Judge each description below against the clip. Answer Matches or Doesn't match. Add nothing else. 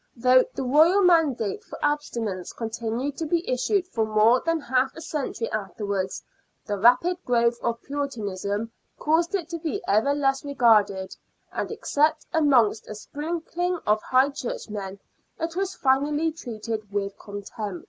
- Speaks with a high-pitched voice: Matches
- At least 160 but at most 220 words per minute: Doesn't match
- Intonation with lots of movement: Matches